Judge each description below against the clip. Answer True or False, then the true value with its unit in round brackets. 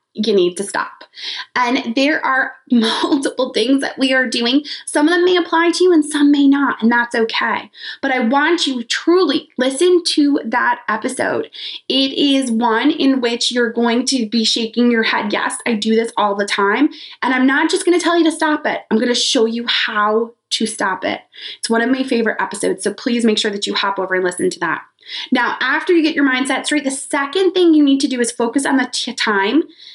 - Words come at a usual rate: False (225 wpm)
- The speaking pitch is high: True (265 Hz)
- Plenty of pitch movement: False (4.9 semitones)